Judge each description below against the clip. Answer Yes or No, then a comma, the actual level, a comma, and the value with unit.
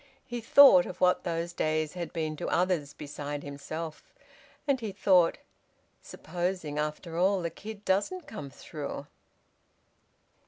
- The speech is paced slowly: Yes, slow, 130 wpm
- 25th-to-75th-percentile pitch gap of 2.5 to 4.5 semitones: Yes, average, 3.9 semitones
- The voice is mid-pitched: Yes, medium, 170 Hz